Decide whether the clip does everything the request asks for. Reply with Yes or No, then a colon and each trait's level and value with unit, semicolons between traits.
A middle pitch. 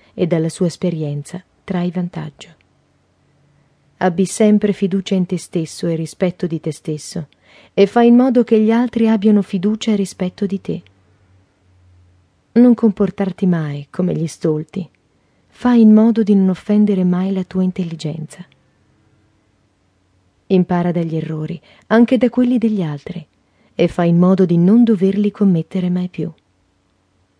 Yes: medium, 180 Hz